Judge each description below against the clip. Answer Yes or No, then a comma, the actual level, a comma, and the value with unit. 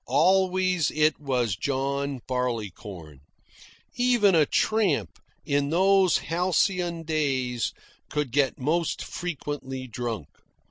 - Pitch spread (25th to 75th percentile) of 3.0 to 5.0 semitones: No, wide, 5.6 semitones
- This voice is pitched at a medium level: Yes, medium, 145 Hz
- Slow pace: Yes, slow, 95 wpm